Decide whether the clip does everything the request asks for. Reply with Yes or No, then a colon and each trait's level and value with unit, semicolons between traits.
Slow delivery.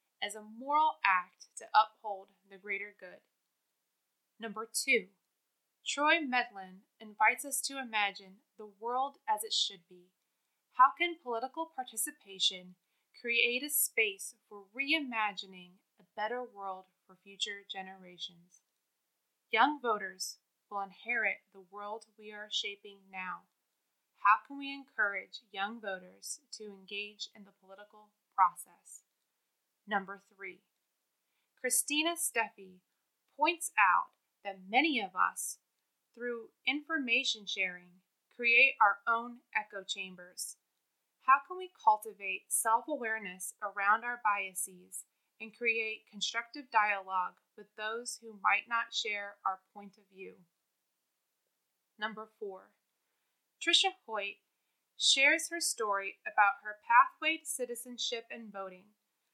Yes: slow, 115 wpm